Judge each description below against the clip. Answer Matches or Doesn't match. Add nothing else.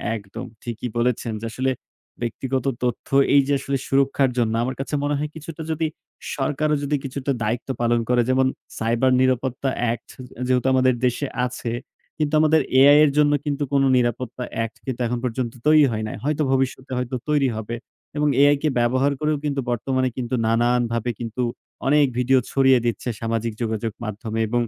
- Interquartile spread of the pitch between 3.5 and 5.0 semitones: Doesn't match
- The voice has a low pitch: Matches